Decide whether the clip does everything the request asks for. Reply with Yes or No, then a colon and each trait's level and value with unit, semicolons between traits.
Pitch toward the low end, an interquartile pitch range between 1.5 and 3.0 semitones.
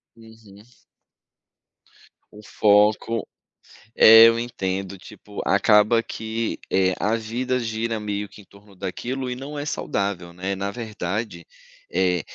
Yes: low, 105 Hz; average, 2.7 semitones